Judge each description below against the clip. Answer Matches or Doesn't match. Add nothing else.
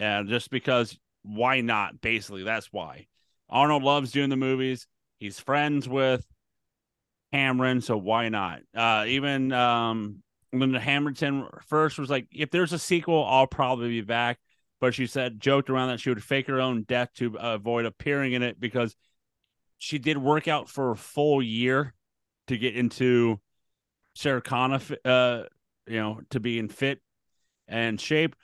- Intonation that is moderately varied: Matches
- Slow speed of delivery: Doesn't match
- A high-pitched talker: Doesn't match